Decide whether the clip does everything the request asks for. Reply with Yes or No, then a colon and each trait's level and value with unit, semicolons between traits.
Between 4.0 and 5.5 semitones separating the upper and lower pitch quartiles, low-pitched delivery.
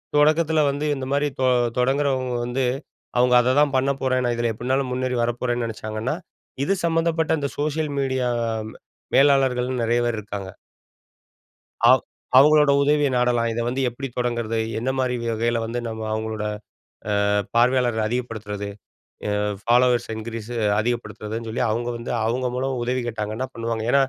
No: average, 2.7 semitones; low, 125 Hz